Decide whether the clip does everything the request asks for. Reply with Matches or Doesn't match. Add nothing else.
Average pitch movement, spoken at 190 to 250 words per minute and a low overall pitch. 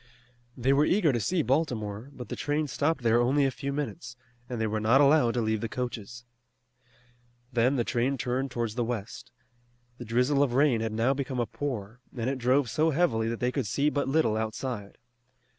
Matches